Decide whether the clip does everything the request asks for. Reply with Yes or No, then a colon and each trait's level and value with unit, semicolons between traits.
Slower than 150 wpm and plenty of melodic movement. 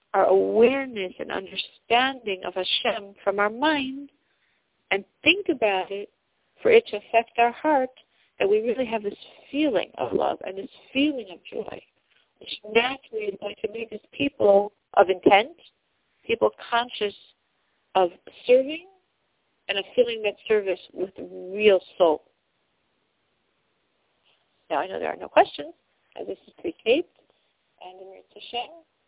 Yes: average, 140 wpm; wide, 6.1 semitones